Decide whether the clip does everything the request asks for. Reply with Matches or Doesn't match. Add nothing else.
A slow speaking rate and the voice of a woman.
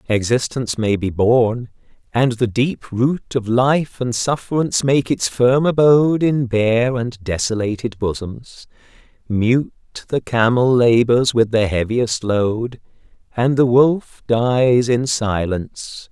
Doesn't match